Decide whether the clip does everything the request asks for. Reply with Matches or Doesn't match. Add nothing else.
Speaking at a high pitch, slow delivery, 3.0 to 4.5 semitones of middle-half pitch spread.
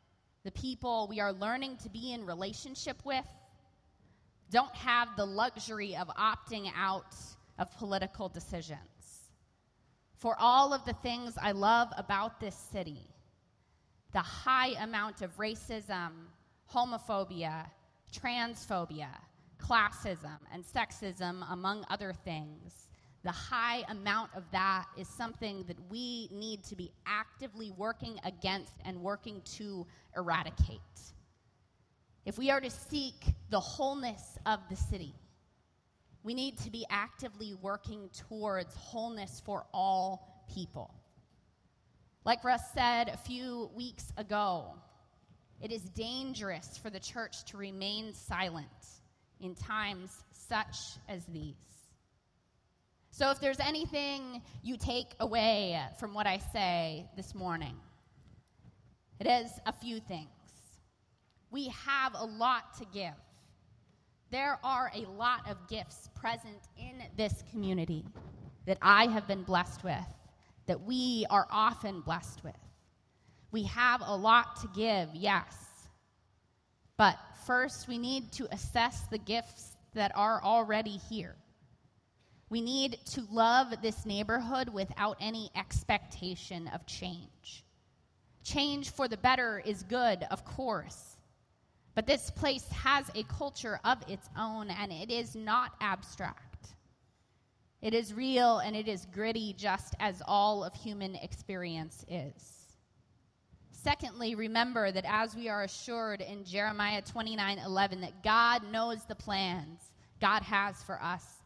Matches